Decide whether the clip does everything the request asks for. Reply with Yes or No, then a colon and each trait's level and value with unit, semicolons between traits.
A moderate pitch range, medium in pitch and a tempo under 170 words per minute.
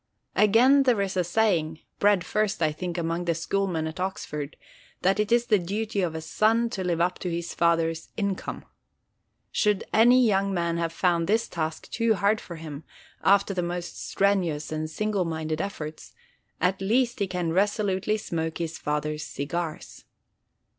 Yes: average, 4.0 semitones; medium, 180 Hz; average, 160 wpm